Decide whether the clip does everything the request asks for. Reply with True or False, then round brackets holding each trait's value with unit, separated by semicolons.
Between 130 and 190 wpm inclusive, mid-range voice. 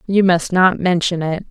False (200 wpm; 180 Hz)